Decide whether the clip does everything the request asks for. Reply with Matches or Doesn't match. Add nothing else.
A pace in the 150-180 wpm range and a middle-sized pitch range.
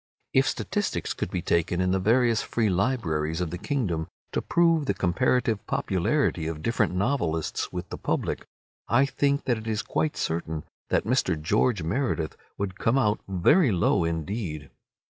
Doesn't match